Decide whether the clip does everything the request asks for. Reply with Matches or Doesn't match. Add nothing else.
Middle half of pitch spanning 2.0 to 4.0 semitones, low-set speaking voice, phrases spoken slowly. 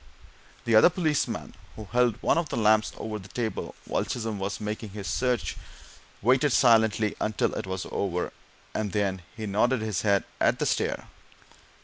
Doesn't match